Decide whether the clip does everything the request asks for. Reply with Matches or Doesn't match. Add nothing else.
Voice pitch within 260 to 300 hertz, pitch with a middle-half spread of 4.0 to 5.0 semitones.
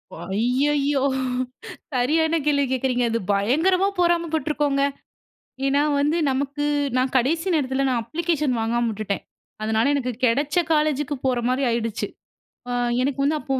Doesn't match